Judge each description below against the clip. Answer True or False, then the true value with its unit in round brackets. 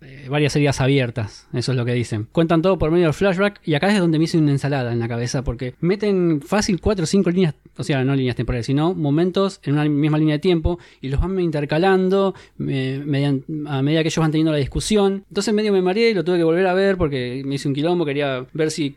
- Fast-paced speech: True (250 wpm)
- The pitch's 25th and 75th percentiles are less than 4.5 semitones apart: False (4.8 semitones)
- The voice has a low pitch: False (155 Hz)